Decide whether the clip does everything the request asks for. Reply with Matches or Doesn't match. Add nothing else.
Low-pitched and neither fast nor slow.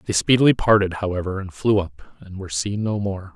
Doesn't match